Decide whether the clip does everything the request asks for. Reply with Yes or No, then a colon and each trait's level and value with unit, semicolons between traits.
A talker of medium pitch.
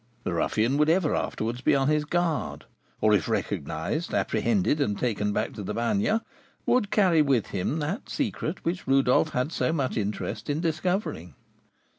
Yes: medium, 145 Hz